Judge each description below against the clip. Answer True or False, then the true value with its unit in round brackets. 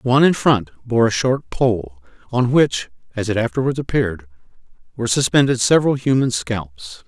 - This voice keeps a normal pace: True (155 wpm)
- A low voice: True (115 Hz)